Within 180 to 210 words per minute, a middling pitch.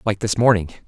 No: fast, 205 wpm; low, 105 Hz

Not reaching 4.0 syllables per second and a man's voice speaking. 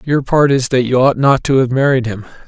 No: 5.5 syllables/s; male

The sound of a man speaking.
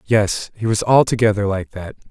Yes: male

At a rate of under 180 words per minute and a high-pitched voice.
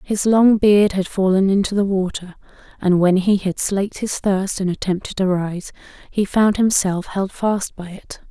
No: average, 190 wpm; high, 195 Hz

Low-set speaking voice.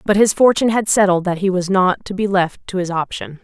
No: high, 190 Hz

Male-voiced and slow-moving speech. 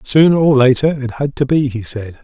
No: male; fast, 240 wpm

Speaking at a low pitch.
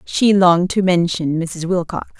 No: medium, 175 Hz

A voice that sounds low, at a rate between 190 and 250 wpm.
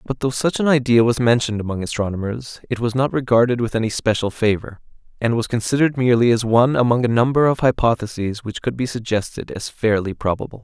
Yes: low, 120 Hz; average, 195 wpm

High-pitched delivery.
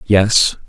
No: low, 100 Hz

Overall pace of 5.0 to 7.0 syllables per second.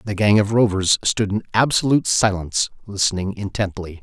Yes: 5.5 syllables/s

